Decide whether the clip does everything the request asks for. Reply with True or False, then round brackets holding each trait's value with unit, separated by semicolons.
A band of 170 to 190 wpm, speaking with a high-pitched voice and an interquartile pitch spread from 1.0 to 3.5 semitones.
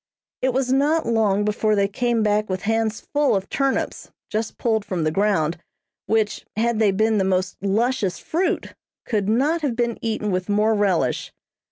True (175 wpm; 215 Hz; 3.1 semitones)